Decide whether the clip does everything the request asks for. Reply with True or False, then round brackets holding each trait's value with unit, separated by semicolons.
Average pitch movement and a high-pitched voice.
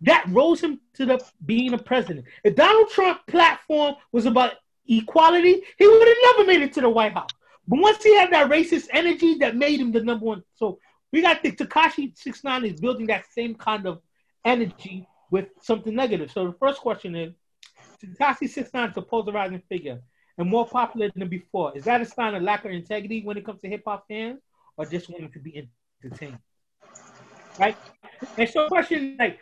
False (6.6 semitones; 235 Hz)